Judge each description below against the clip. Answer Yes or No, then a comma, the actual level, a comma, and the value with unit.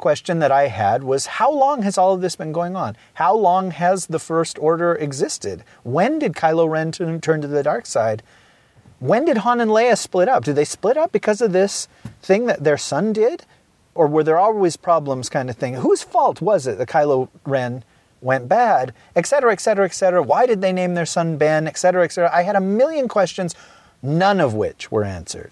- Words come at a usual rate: No, fast, 215 wpm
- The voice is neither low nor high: Yes, medium, 170 Hz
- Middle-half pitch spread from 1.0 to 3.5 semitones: No, average, 5.1 semitones